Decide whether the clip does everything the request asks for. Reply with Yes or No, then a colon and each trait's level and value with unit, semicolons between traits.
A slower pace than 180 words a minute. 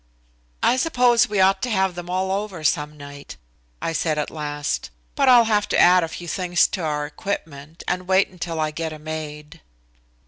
No: average, 195 wpm